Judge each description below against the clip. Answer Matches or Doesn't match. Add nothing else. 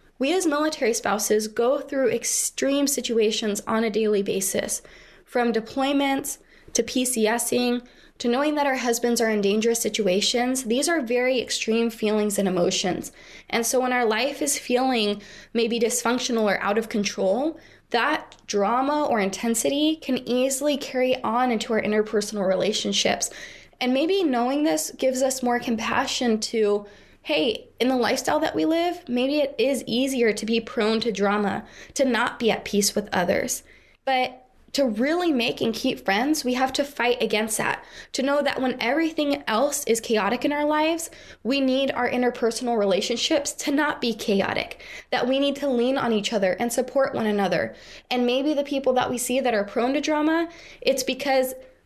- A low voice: Doesn't match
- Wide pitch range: Doesn't match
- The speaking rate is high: Doesn't match